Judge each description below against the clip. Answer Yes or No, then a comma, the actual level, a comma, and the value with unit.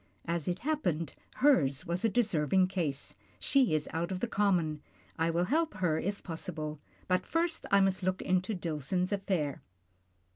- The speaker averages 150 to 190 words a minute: Yes, average, 170 wpm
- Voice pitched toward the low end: No, medium, 180 Hz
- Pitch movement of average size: Yes, average, 3.8 semitones